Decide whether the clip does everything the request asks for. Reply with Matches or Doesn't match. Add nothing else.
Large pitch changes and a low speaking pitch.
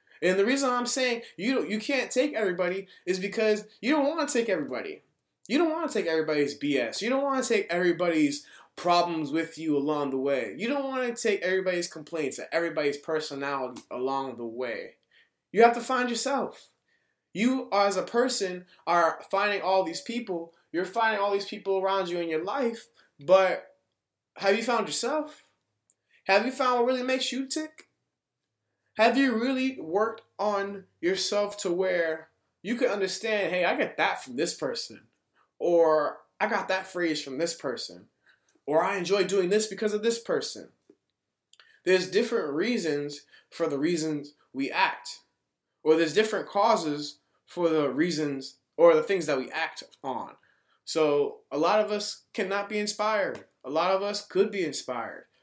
Doesn't match